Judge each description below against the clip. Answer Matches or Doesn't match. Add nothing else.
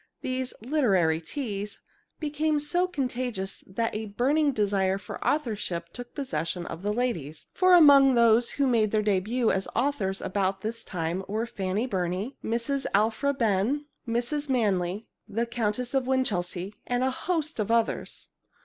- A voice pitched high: Matches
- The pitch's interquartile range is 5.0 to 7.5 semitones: Matches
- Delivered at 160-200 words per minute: Doesn't match